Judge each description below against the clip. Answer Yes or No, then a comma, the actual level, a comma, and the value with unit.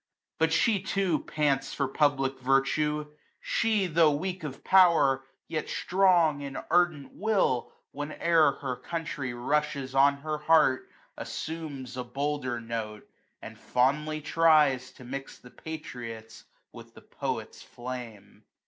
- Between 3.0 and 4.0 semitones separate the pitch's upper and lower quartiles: Yes, average, 3.7 semitones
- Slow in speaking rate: Yes, slow, 130 wpm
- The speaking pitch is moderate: Yes, medium, 145 Hz